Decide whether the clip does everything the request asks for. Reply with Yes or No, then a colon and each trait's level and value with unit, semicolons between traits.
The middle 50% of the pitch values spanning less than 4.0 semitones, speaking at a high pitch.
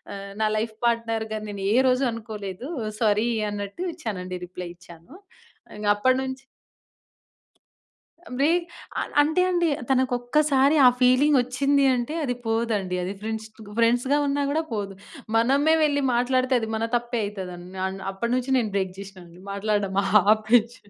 No: average, 4.4 semitones; high, 230 Hz